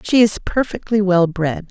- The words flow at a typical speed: Yes, average, 175 wpm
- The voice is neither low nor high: No, high, 195 Hz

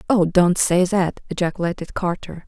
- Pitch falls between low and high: Yes, medium, 180 Hz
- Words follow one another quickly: No, average, 145 wpm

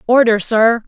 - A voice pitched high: Yes, high, 230 Hz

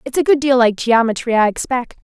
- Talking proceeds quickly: Yes, fast, 220 wpm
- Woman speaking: Yes, female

